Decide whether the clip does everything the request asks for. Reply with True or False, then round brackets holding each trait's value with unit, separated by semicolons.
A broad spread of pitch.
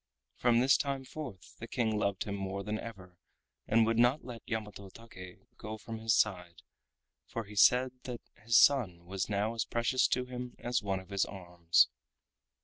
False (3.7 semitones)